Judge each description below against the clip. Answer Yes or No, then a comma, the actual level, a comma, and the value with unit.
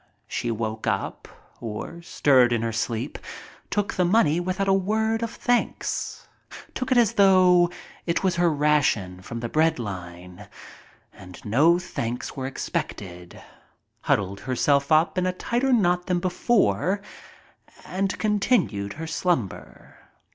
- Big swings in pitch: Yes, wide, 8.9 semitones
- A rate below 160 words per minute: Yes, average, 140 wpm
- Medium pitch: Yes, medium, 160 Hz